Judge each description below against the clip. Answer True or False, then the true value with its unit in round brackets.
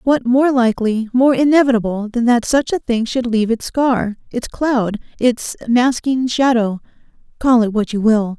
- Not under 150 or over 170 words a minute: True (165 wpm)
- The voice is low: False (240 Hz)